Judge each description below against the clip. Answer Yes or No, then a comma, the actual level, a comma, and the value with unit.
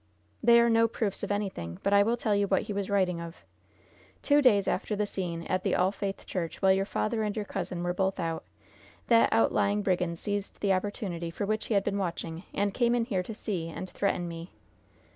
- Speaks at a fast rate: Yes, fast, 220 wpm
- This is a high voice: Yes, high, 200 Hz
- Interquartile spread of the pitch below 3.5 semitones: Yes, average, 2.8 semitones